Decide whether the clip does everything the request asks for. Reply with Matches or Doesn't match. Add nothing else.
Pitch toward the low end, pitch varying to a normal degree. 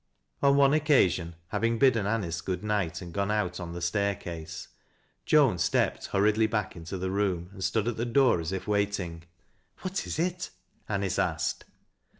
Matches